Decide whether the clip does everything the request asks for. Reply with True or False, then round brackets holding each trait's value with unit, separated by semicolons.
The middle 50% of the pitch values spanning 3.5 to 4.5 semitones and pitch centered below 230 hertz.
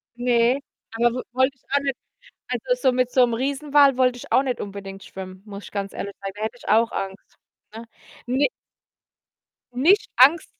False (4.0 semitones; 245 Hz)